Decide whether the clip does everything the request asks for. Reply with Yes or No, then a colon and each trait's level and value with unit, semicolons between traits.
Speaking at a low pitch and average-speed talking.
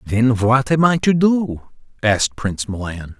Yes: low, 120 Hz; average, 170 wpm